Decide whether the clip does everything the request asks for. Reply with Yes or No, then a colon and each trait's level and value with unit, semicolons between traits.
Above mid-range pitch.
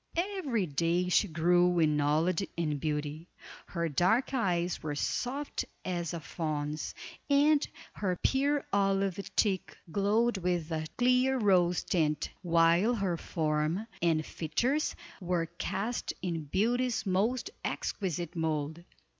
No: medium, 180 Hz